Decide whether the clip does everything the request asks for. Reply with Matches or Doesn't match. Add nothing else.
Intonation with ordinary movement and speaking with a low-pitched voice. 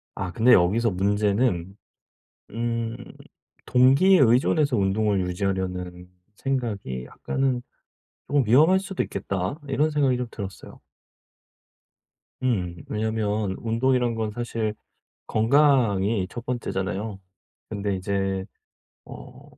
Matches